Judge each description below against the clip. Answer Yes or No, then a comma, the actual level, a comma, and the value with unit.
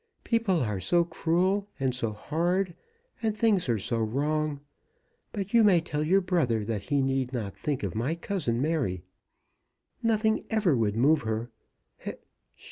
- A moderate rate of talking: Yes, average, 150 wpm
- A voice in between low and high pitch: Yes, medium, 150 Hz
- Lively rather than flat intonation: Yes, wide, 8.1 semitones